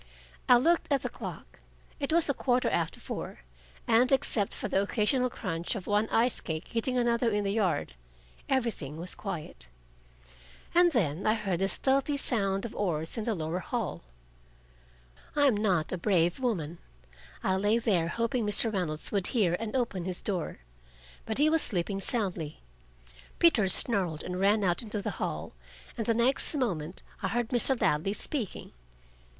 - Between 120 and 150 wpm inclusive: No, average, 165 wpm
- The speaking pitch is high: Yes, high, 210 Hz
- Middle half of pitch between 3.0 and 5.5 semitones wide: Yes, average, 5.1 semitones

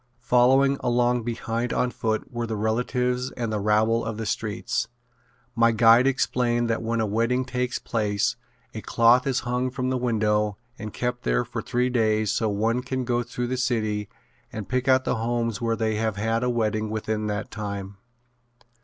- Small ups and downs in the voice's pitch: Yes, narrow, 2.3 semitones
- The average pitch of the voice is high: No, low, 115 Hz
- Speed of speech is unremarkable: Yes, average, 180 wpm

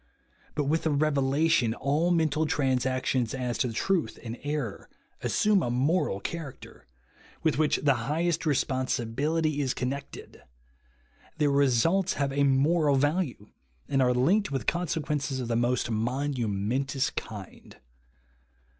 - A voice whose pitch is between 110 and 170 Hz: Yes, medium, 140 Hz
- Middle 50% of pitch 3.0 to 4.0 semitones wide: Yes, average, 3.7 semitones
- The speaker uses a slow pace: Yes, slow, 125 wpm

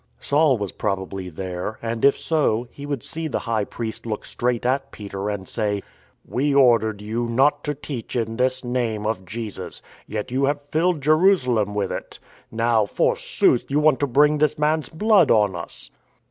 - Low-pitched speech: Yes, low, 120 Hz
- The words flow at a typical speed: Yes, average, 180 wpm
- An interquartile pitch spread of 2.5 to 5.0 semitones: No, wide, 5.4 semitones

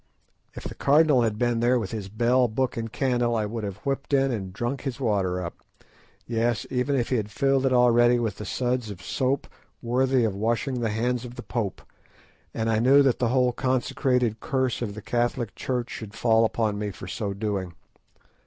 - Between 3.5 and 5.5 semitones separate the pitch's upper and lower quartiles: No, average, 2.8 semitones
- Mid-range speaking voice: No, low, 120 Hz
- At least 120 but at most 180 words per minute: No, average, 200 wpm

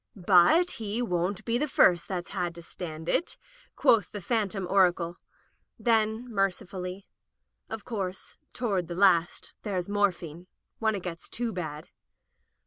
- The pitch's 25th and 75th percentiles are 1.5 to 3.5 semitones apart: No, average, 3.9 semitones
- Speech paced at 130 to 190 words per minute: Yes, average, 140 wpm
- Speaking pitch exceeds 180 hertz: Yes, high, 190 Hz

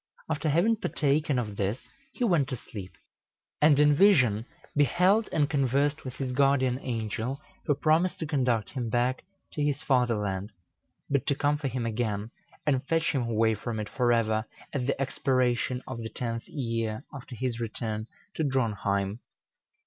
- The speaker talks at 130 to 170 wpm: Yes, average, 160 wpm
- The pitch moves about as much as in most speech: Yes, average, 4.1 semitones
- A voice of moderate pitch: No, low, 130 Hz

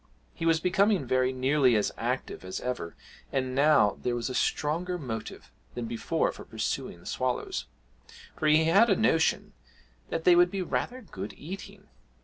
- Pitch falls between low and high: Yes, medium, 150 Hz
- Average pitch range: No, wide, 6.0 semitones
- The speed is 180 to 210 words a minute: No, average, 165 wpm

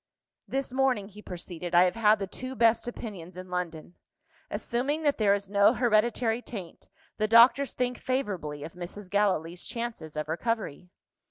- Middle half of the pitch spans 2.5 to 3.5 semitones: No, average, 5.0 semitones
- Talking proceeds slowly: No, average, 160 wpm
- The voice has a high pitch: Yes, high, 210 Hz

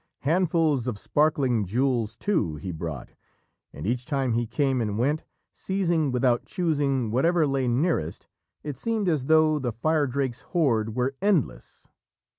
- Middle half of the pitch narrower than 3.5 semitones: No, average, 5.0 semitones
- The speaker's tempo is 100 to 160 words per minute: Yes, average, 140 wpm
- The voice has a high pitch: No, low, 135 Hz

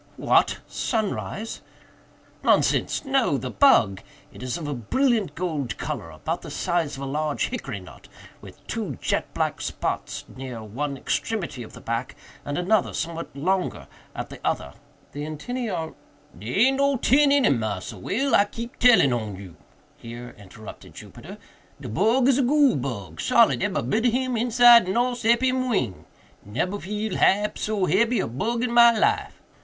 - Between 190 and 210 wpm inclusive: No, average, 165 wpm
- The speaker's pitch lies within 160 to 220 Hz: Yes, medium, 185 Hz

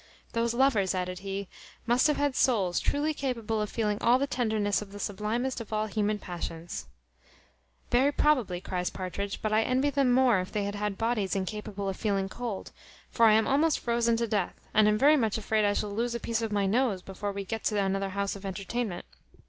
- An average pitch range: Yes, average, 3.3 semitones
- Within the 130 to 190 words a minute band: No, fast, 205 wpm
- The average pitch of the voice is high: Yes, high, 215 Hz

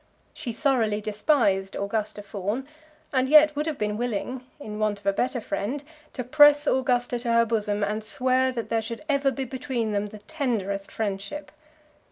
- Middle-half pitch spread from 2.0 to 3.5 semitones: No, average, 4.1 semitones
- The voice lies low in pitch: No, high, 230 Hz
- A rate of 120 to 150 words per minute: No, average, 175 wpm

